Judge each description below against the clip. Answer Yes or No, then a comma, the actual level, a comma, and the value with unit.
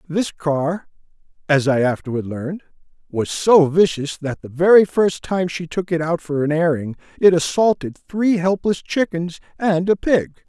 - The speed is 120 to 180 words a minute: Yes, average, 165 wpm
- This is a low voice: No, medium, 170 Hz